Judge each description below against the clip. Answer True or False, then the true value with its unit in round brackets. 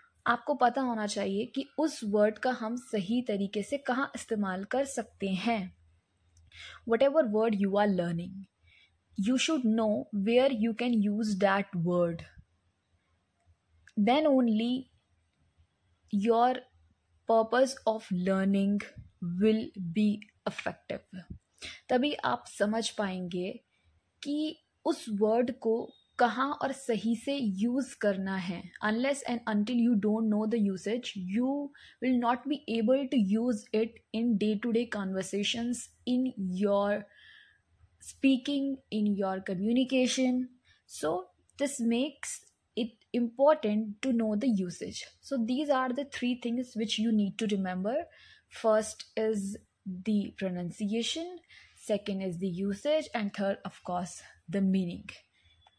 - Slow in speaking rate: True (125 wpm)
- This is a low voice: False (220 Hz)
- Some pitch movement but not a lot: True (4.4 semitones)